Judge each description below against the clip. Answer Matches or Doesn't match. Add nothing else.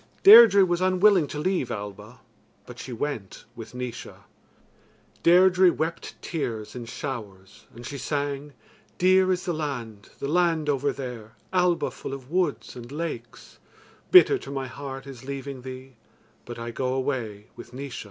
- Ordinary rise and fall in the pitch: Doesn't match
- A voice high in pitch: Doesn't match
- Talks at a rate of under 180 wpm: Matches